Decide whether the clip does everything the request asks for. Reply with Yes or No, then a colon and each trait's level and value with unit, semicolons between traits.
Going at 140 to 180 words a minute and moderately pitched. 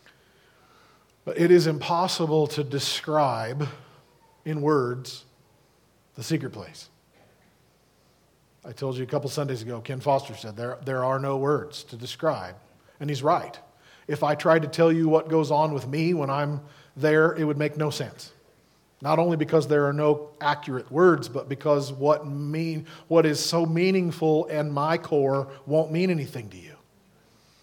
Yes: average, 160 wpm; medium, 150 Hz